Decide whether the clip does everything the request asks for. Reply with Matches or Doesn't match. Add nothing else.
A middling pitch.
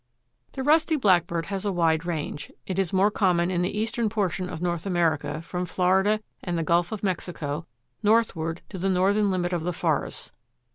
Matches